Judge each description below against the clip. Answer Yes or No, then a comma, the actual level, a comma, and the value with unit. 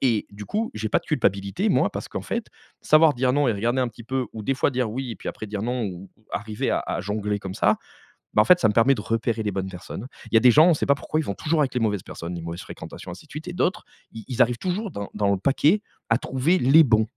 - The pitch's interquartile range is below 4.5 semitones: No, average, 5.0 semitones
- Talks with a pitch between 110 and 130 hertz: Yes, low, 115 Hz